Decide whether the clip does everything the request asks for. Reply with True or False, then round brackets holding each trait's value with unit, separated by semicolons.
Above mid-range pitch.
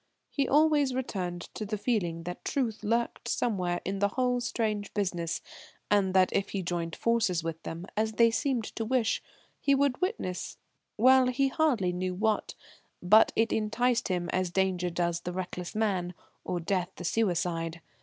True (200 Hz)